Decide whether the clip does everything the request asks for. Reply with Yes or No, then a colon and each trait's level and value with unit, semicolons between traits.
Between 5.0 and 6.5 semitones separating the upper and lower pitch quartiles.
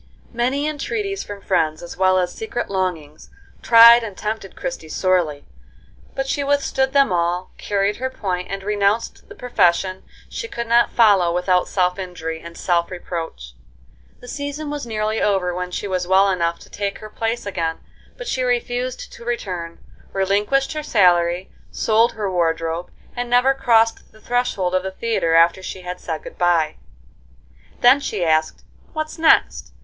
Yes: average, 5.3 semitones